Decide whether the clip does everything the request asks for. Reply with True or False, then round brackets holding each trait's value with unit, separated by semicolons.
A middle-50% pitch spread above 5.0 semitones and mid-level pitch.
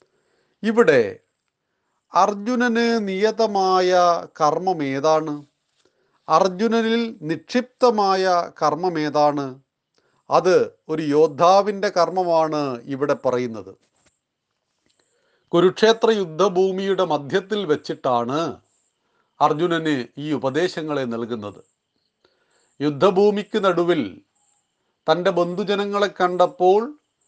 True (5.5 semitones; 180 Hz)